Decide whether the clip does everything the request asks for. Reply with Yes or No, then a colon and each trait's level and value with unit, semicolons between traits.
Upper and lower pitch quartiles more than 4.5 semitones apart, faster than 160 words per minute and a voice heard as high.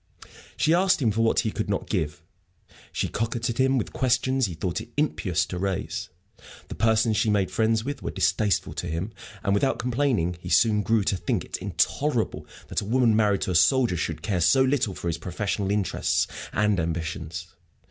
No: average, 4.9 semitones; average, 190 wpm; low, 105 Hz